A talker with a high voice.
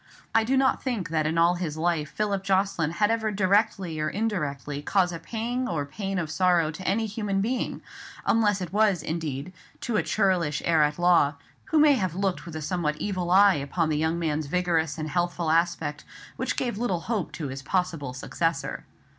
No: medium, 175 Hz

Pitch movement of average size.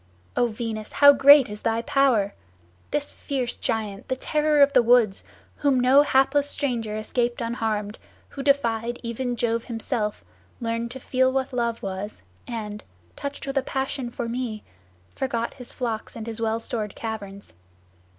Yes: average, 3.2 semitones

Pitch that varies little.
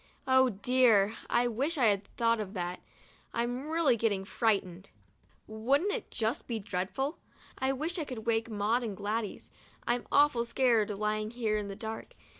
No: average, 3.6 semitones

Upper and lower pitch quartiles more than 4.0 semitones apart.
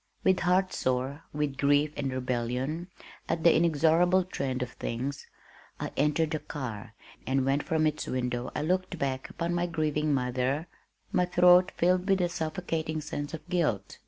Yes: average, 4.7 semitones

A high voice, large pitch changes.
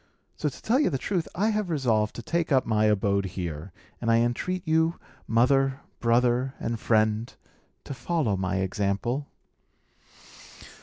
No: low, 120 Hz; wide, 6.6 semitones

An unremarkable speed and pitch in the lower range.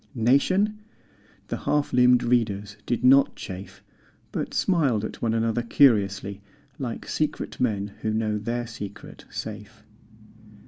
No: slow, 125 wpm; low, 115 Hz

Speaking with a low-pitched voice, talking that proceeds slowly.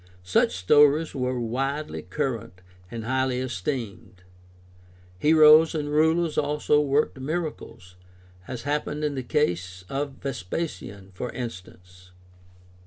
Yes: low, 130 Hz; slow, 105 wpm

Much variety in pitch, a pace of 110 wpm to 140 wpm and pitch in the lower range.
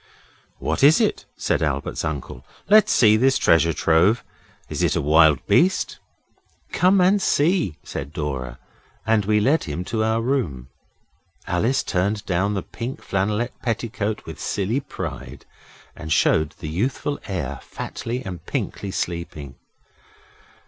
Yes: wide, 7.3 semitones; slow, 135 wpm; low, 100 Hz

